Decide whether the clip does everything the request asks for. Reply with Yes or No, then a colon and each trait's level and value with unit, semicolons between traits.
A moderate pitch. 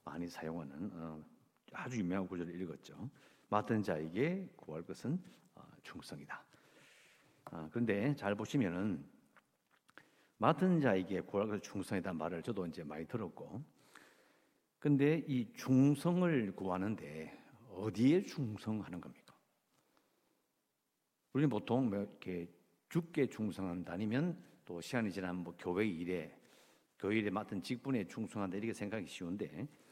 No: low, 105 Hz